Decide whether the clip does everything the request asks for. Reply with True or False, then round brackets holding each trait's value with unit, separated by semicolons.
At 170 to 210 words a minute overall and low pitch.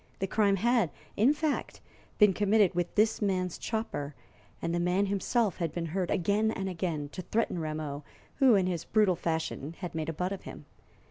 False (190 wpm; 185 Hz)